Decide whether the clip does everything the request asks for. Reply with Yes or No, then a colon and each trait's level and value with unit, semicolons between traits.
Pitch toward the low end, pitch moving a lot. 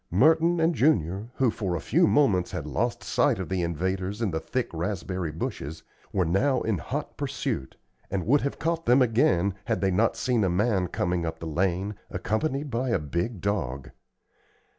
Yes: low, 100 Hz; wide, 6.2 semitones